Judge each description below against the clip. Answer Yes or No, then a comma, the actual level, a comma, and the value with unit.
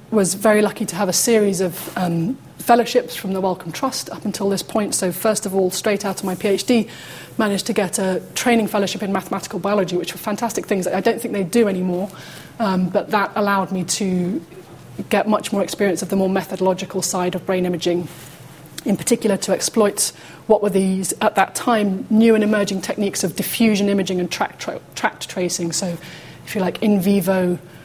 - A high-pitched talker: Yes, high, 195 Hz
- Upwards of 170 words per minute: Yes, average, 200 wpm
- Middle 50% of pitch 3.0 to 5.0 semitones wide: No, narrow, 2.6 semitones